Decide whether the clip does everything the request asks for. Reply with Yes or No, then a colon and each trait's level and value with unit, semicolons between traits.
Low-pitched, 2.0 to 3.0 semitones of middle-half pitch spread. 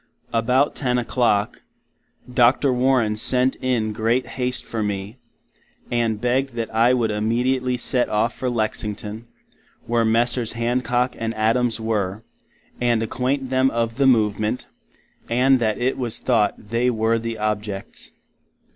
Yes: low, 115 Hz; narrow, 2.4 semitones